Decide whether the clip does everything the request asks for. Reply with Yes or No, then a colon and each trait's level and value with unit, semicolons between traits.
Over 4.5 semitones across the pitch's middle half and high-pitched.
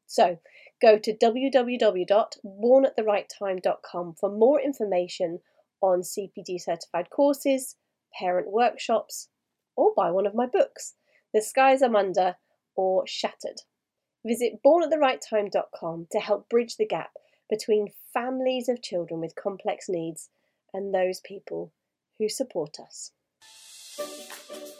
Yes: wide, 5.5 semitones; high, 215 Hz